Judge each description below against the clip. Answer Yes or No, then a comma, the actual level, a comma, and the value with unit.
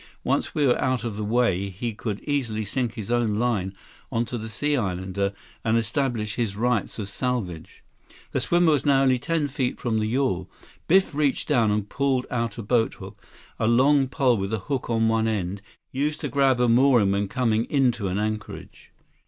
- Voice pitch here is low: Yes, low, 115 Hz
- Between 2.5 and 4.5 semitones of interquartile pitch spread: Yes, average, 3.8 semitones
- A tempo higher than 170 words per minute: Yes, average, 190 wpm